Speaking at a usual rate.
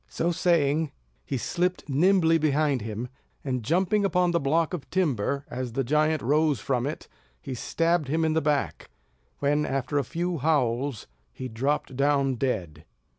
Yes: average, 160 wpm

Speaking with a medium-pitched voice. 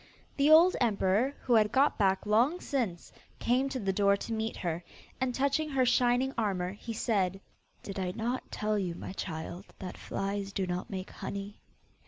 No: high, 210 Hz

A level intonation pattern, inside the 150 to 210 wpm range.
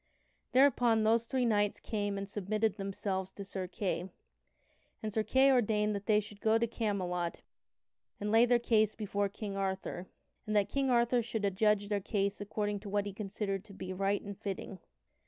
Yes: narrow, 2.0 semitones; average, 180 wpm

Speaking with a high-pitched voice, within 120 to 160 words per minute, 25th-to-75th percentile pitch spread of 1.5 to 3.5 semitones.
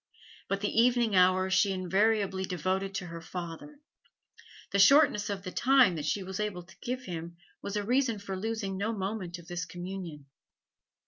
No: high, 195 Hz; average, 175 wpm; average, 2.9 semitones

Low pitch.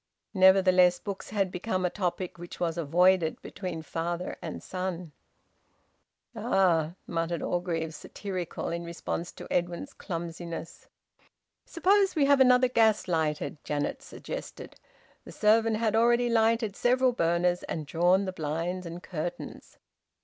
No: medium, 180 Hz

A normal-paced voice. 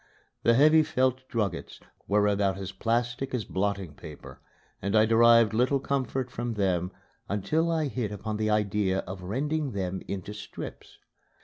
Yes: average, 150 wpm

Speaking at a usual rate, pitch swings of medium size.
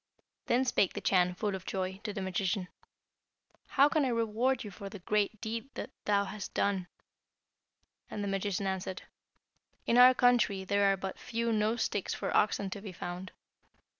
Yes: average, 175 wpm; average, 3.1 semitones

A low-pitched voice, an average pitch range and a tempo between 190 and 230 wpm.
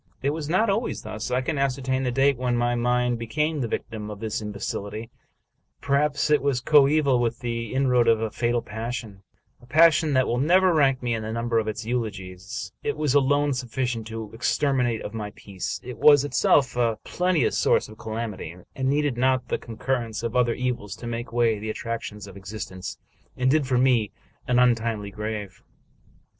Yes: low, 120 Hz; average, 3.4 semitones; average, 200 wpm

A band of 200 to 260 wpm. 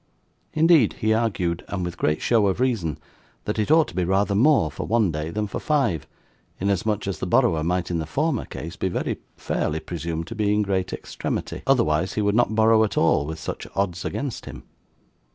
Yes: fast, 205 wpm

